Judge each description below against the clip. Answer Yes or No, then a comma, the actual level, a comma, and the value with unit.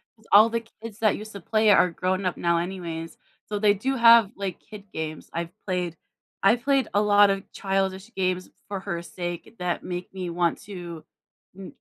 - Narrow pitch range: No, average, 3.0 semitones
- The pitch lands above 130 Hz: Yes, high, 190 Hz